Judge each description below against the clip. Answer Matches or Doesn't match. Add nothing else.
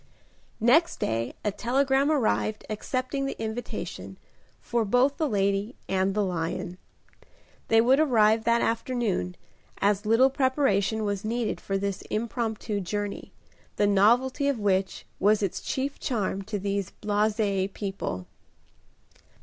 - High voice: Matches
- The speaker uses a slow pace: Matches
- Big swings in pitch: Doesn't match